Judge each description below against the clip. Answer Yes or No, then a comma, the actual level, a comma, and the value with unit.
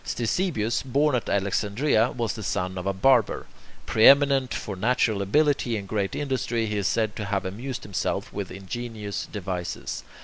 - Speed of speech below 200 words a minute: Yes, average, 160 wpm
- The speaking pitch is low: Yes, low, 110 Hz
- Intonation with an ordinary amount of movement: Yes, average, 4.2 semitones